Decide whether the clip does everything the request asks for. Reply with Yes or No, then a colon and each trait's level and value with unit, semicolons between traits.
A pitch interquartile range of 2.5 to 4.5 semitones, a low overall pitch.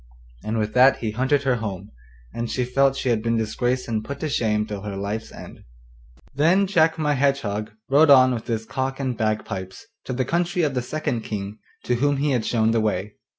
Yes: average, 4.2 semitones; low, 120 Hz